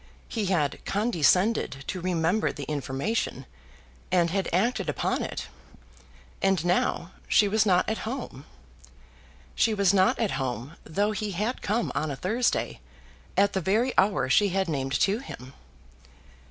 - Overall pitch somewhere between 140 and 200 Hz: Yes, high, 190 Hz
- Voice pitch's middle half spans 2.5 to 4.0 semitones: No, average, 5.0 semitones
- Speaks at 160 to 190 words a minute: No, average, 145 wpm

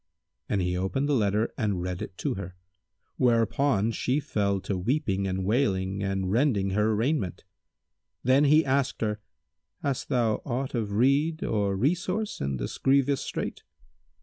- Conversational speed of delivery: Yes, average, 150 wpm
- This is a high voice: No, low, 110 Hz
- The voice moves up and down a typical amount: No, wide, 6.0 semitones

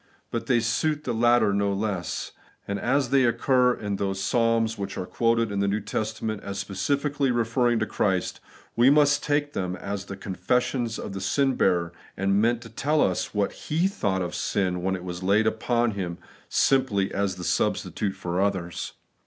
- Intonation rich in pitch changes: No, average, 3.9 semitones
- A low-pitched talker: Yes, low, 105 Hz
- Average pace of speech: Yes, average, 185 wpm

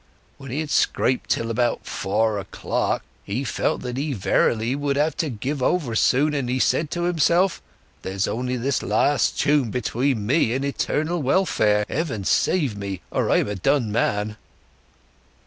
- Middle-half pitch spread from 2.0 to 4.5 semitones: No, average, 5.1 semitones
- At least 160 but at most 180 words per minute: Yes, average, 165 wpm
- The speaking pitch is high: No, low, 125 Hz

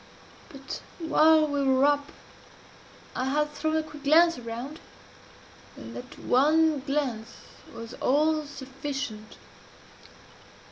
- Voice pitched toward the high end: Yes, very high, 285 Hz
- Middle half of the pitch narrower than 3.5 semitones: Yes, average, 2.8 semitones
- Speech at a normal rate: No, slow, 105 wpm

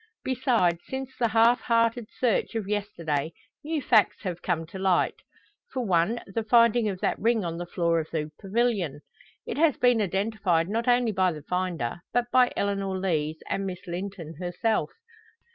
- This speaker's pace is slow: No, average, 170 wpm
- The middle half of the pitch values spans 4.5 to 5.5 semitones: Yes, average, 5.1 semitones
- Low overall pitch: No, high, 195 Hz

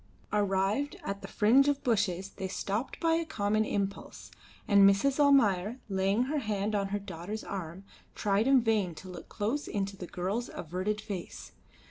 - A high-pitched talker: Yes, high, 205 Hz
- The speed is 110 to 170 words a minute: Yes, average, 165 wpm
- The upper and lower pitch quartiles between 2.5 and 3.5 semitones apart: Yes, average, 2.9 semitones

